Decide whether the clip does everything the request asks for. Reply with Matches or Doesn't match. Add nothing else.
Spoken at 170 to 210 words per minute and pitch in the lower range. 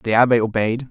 Matches